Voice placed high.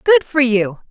Yes: very high, 260 Hz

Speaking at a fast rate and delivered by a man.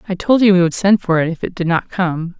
No: fast, 325 wpm; female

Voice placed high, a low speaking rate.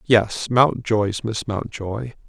No: low, 110 Hz; slow, 105 wpm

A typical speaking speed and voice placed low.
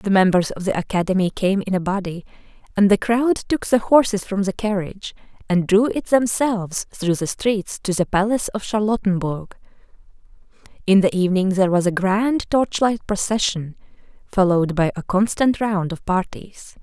No: average, 165 wpm; high, 200 Hz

